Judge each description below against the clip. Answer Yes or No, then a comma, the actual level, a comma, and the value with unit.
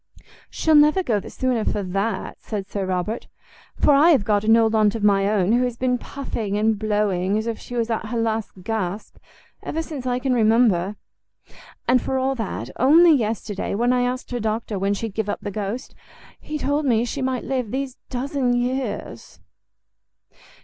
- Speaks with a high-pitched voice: Yes, high, 225 Hz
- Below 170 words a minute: No, average, 190 wpm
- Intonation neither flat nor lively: Yes, average, 3.6 semitones